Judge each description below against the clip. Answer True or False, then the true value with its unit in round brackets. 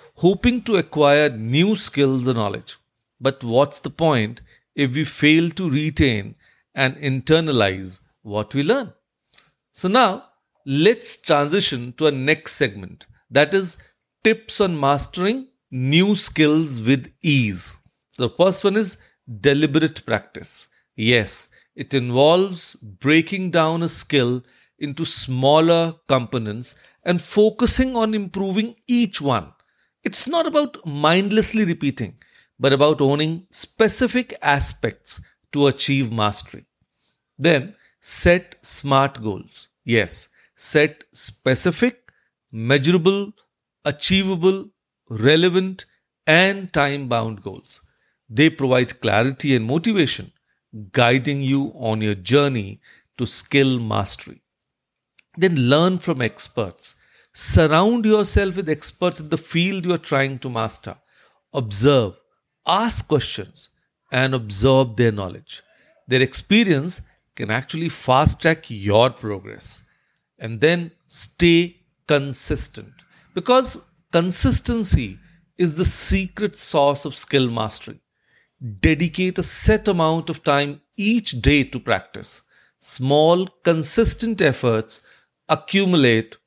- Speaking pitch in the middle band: True (145 Hz)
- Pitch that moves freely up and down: True (5.9 semitones)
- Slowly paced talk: True (110 wpm)